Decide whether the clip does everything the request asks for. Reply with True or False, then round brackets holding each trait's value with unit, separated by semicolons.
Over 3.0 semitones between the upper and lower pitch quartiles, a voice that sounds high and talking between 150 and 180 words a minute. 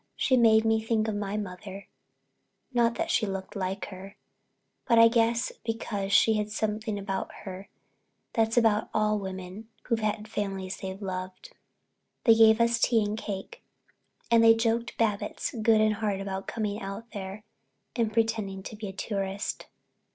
False (2.5 semitones; 215 Hz; 160 wpm)